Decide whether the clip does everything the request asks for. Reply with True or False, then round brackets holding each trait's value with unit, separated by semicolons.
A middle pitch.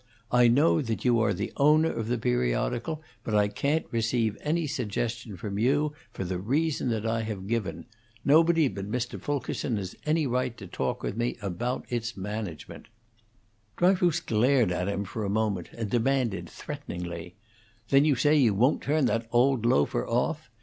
False (115 Hz)